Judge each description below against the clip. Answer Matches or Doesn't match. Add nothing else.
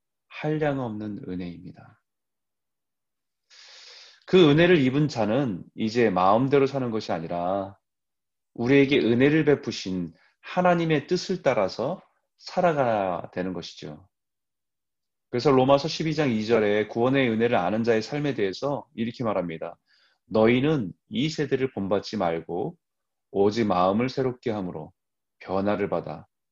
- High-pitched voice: Doesn't match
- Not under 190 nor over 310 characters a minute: Matches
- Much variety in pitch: Matches